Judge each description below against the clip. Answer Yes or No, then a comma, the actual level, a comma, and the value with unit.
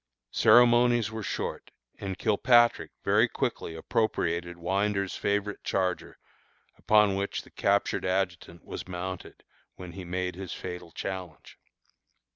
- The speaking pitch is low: Yes, very low, 95 Hz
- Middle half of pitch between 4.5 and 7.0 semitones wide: No, average, 2.7 semitones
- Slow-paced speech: Yes, slow, 115 wpm